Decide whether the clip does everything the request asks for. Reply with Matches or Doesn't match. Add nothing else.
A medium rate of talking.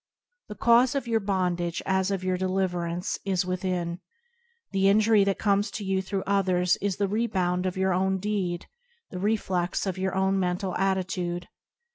Matches